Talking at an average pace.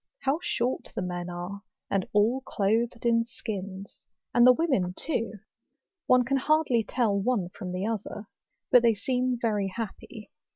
Yes: average, 155 wpm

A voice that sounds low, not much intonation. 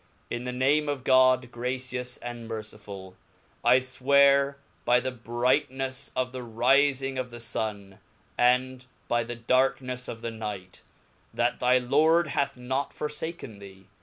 Yes: low, 125 Hz; narrow, 2.0 semitones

